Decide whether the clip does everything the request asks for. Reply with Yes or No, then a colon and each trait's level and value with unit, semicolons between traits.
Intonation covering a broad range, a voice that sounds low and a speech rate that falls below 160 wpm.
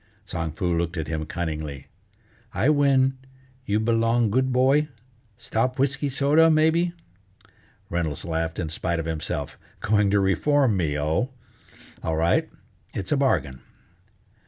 Yes: wide, 8.5 semitones; low, 100 Hz; slow, 135 wpm